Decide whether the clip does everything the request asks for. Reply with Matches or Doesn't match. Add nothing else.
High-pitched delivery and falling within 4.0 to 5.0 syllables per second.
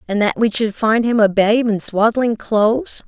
Matches